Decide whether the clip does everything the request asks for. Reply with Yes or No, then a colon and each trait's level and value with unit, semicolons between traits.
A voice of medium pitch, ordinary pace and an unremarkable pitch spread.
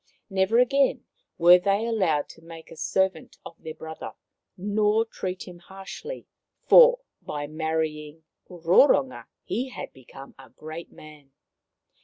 No: medium, 175 Hz; slow, 130 wpm; average, 4.9 semitones